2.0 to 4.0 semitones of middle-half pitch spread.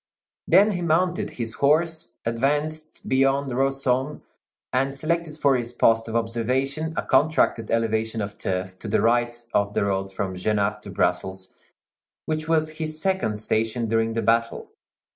No: wide, 5.6 semitones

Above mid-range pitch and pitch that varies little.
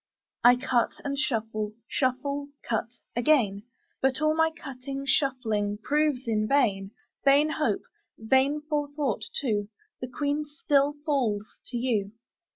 No: very high, 260 Hz; average, 4.5 semitones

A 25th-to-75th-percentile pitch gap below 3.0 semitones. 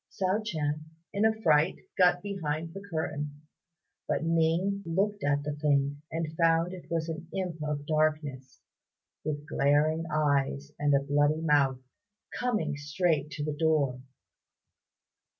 Yes: narrow, 2.4 semitones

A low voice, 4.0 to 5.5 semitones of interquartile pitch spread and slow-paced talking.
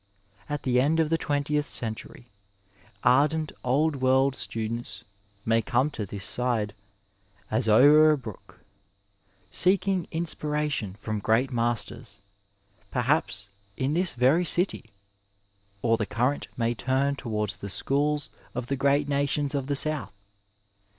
Yes: low, 130 Hz; average, 4.4 semitones; slow, 130 wpm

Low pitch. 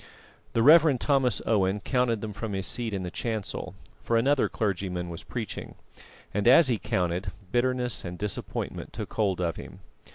Yes: low, 110 Hz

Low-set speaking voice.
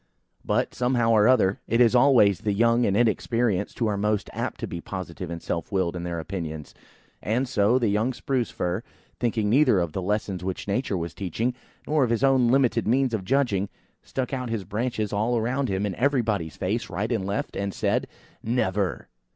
Yes: low, 105 Hz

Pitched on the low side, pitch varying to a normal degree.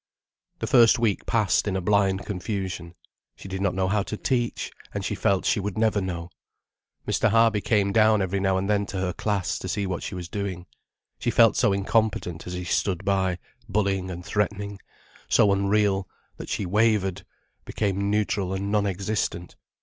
No: low, 100 Hz; narrow, 2.1 semitones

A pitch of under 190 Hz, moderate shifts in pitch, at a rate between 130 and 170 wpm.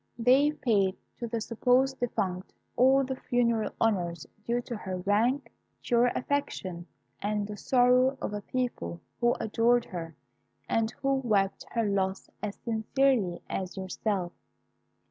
No: high, 225 Hz; average, 4.4 semitones; average, 140 wpm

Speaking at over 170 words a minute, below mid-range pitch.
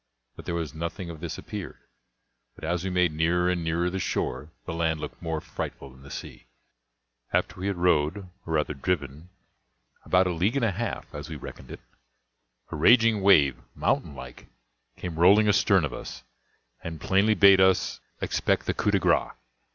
Yes: average, 180 wpm; very low, 85 Hz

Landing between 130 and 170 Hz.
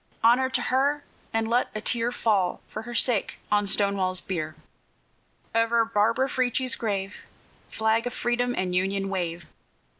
No: high, 225 Hz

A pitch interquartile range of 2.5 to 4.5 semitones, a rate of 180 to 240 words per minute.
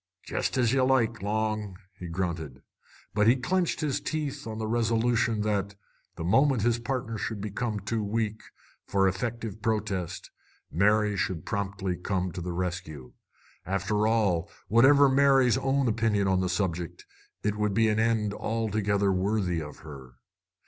No: average, 3.5 semitones; average, 150 wpm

